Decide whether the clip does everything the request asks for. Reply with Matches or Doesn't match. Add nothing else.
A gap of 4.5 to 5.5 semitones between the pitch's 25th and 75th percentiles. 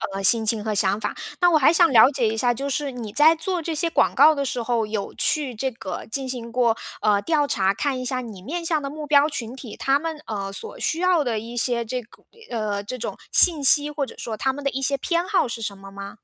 Matches